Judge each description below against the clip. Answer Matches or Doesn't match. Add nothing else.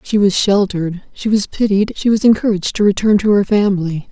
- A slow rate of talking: Doesn't match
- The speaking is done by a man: Doesn't match